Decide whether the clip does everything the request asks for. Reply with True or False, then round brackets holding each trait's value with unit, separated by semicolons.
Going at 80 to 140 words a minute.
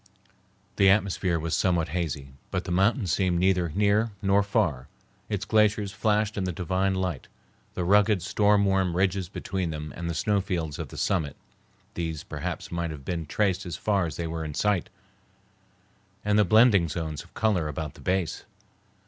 False (175 wpm)